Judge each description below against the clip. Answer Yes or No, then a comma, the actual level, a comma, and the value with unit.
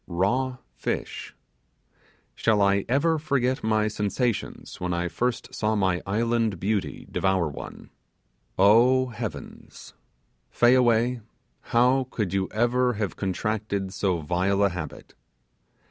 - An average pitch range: Yes, average, 4.3 semitones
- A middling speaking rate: No, slow, 115 wpm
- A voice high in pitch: No, low, 105 Hz